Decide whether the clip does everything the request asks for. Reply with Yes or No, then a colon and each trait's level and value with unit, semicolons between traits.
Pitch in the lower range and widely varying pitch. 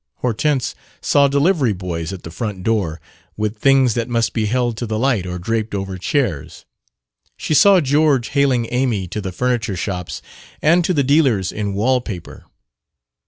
Yes: low, 115 Hz; wide, 5.7 semitones